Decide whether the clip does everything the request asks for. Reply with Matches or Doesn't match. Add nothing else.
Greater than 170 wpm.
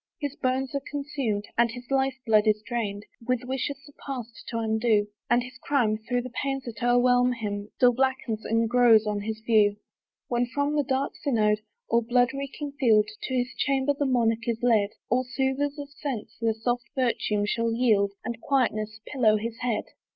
Matches